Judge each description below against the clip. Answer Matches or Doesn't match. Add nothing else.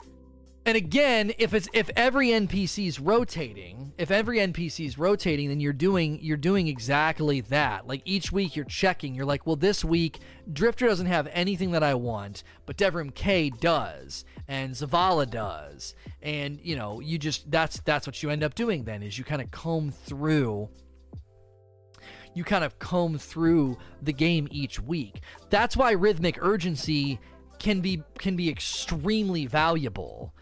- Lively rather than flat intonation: Matches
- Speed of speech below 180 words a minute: Matches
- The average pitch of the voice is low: Doesn't match